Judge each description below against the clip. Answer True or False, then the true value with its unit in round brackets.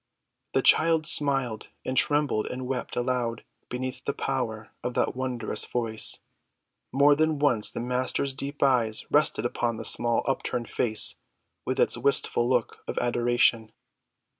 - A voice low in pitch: True (125 Hz)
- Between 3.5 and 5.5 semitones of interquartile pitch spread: False (2.6 semitones)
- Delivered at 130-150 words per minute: True (140 wpm)